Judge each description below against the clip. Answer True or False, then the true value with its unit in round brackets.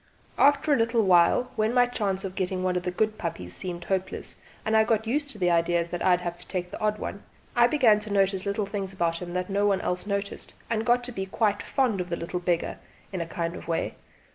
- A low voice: False (195 Hz)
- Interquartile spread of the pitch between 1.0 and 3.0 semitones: False (3.6 semitones)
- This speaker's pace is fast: True (250 wpm)